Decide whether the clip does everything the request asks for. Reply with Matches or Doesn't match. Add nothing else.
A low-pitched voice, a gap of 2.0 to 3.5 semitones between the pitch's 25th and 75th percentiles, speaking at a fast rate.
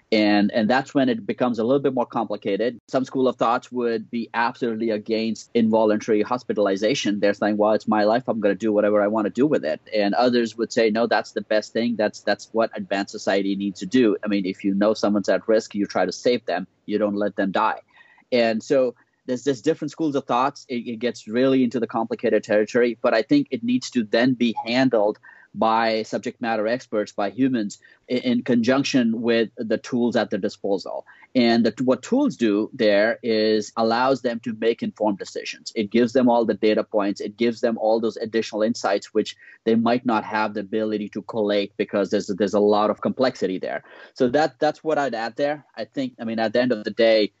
Matches